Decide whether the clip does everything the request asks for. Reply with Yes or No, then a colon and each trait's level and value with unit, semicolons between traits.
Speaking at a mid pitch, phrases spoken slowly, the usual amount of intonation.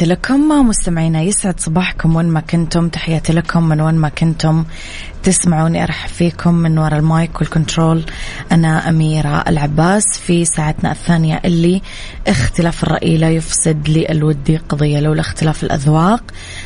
No: medium, 165 Hz; slow, 130 wpm; narrow, 1.6 semitones